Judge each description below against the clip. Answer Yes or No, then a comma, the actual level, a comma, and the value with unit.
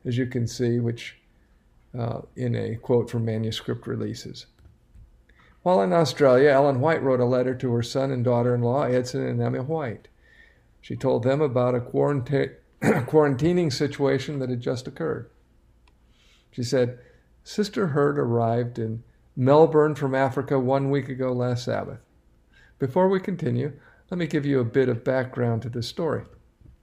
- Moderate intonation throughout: Yes, average, 3.0 semitones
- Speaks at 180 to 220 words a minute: No, average, 160 wpm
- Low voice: Yes, low, 130 Hz